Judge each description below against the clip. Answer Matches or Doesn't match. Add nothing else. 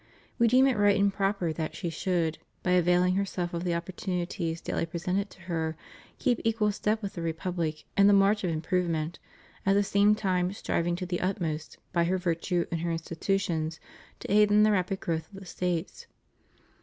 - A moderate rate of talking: Matches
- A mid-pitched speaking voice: Matches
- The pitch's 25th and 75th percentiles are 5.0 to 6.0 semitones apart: Doesn't match